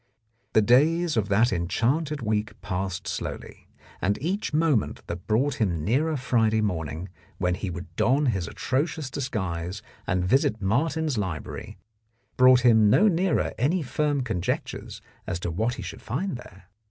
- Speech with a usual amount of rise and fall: No, wide, 7.2 semitones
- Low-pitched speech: Yes, low, 110 Hz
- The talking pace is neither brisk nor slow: Yes, average, 150 wpm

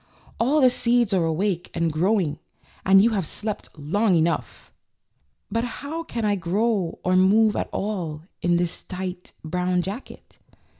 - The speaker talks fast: No, average, 155 wpm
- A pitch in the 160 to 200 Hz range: Yes, high, 190 Hz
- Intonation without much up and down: No, average, 4.2 semitones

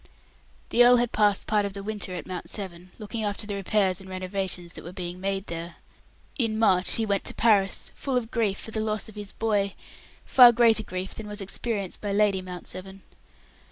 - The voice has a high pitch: Yes, high, 200 Hz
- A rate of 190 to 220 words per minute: Yes, fast, 205 wpm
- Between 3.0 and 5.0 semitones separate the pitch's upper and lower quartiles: No, narrow, 2.6 semitones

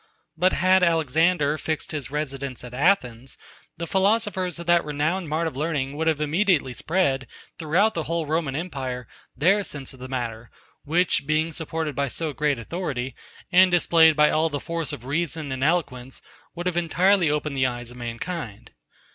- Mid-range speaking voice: Yes, medium, 155 Hz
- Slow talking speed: No, average, 165 wpm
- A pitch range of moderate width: Yes, average, 4.2 semitones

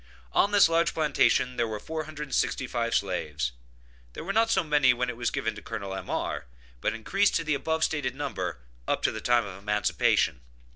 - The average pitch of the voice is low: Yes, low, 125 Hz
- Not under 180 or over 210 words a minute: Yes, average, 185 wpm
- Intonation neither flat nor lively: No, wide, 6.6 semitones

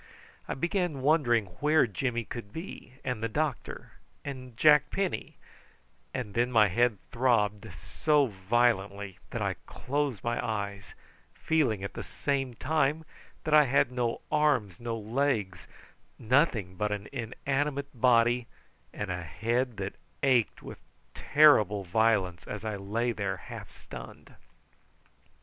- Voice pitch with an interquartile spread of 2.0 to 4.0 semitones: No, average, 5.1 semitones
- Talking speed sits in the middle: No, slow, 130 wpm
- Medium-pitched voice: No, low, 120 Hz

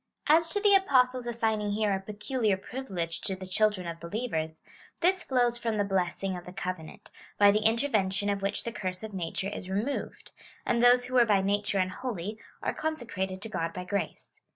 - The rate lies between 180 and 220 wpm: Yes, average, 190 wpm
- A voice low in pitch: No, high, 205 Hz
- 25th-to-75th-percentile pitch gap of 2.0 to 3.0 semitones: No, average, 4.3 semitones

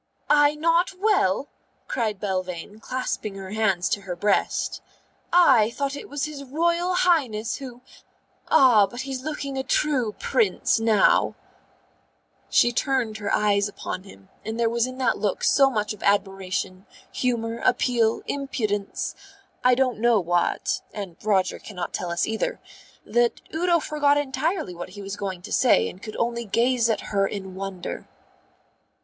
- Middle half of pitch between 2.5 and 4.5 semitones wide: No, average, 5.2 semitones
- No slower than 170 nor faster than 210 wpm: No, average, 155 wpm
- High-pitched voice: Yes, high, 230 Hz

